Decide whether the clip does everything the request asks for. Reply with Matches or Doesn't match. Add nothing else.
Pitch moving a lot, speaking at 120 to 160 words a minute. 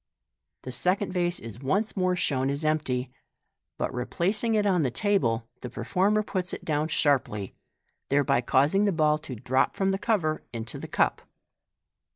Doesn't match